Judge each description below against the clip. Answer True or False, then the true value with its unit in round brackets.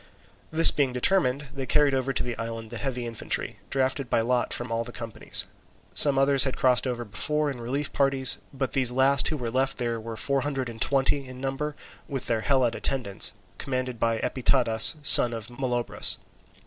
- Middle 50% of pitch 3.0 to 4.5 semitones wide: False (2.5 semitones)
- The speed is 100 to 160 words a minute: False (185 wpm)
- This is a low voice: True (130 Hz)